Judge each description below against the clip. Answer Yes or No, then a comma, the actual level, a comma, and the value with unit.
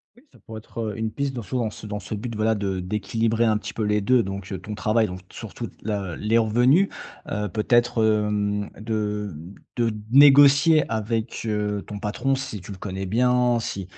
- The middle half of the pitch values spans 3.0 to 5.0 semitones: No, narrow, 2.5 semitones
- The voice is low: Yes, low, 110 Hz